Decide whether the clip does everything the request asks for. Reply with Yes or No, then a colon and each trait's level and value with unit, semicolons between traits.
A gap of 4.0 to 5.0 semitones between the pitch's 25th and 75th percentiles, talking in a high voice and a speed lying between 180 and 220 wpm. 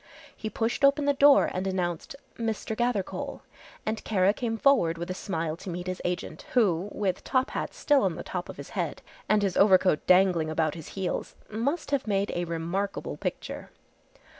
Yes: average, 4.3 semitones; high, 195 Hz; average, 185 wpm